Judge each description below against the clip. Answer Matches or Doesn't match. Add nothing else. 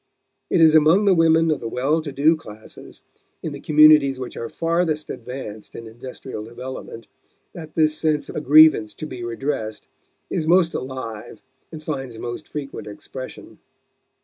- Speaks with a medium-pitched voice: Matches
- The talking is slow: Doesn't match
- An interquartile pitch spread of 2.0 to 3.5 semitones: Doesn't match